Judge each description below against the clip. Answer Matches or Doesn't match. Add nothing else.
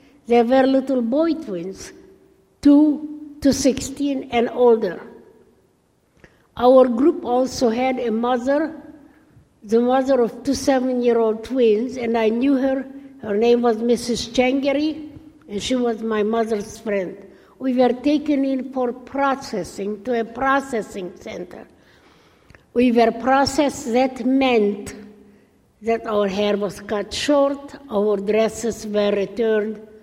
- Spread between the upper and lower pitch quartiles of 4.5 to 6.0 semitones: Doesn't match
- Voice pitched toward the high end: Matches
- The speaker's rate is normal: Doesn't match